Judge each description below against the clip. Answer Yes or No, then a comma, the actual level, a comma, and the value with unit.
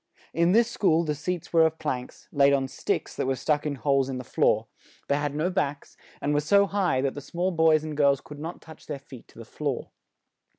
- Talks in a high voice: No, medium, 150 Hz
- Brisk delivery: Yes, fast, 230 wpm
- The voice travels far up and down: No, average, 2.9 semitones